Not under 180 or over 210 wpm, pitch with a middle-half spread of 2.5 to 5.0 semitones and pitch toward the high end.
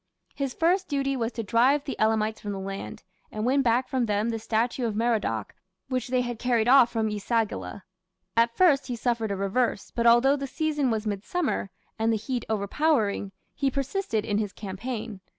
Yes: average, 190 wpm; average, 3.6 semitones; high, 235 Hz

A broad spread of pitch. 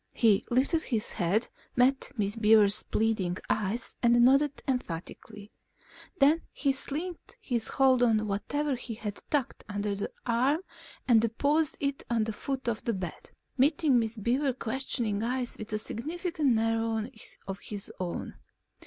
No: average, 4.2 semitones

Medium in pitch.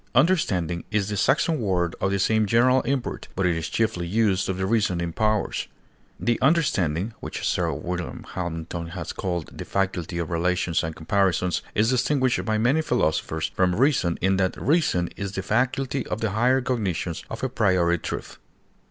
No: very low, 95 Hz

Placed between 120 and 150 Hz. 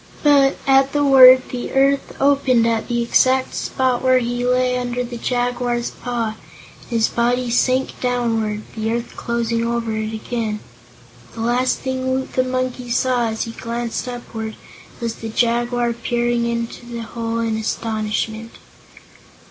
No: high, 240 Hz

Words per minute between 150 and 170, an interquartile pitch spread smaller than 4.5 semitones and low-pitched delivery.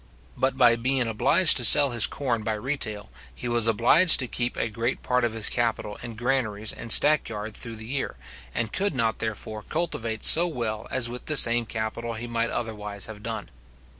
No: average, 200 wpm; narrow, 2.6 semitones; low, 115 Hz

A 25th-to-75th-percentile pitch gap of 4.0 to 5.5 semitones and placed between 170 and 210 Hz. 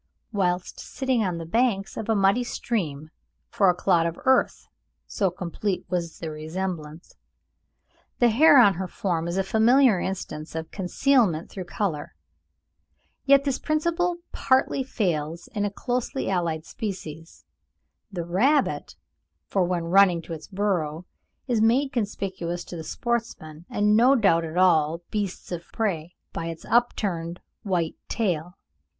Yes: average, 5.2 semitones; high, 190 Hz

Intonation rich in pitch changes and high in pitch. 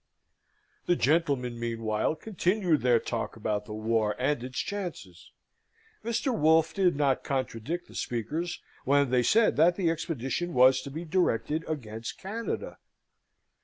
No: wide, 6.6 semitones; medium, 145 Hz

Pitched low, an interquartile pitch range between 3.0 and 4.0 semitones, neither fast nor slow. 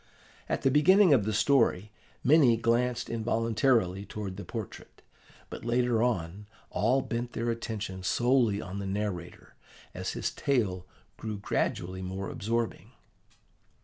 No: low, 110 Hz; average, 3.7 semitones; slow, 130 wpm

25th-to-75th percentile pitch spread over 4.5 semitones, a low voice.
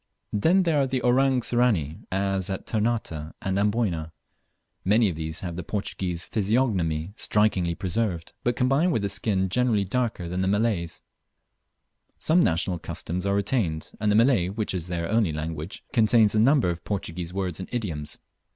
Yes: average, 5.1 semitones; low, 100 Hz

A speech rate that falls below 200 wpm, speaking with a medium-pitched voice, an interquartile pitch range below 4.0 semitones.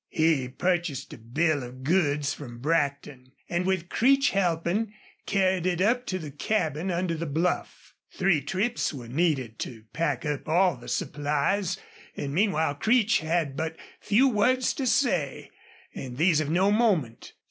No: average, 155 wpm; medium, 165 Hz; average, 5.0 semitones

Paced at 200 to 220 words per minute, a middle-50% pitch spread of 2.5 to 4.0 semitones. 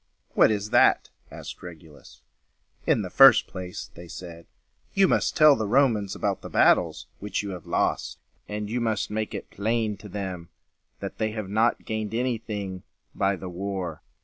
No: average, 175 wpm; average, 3.1 semitones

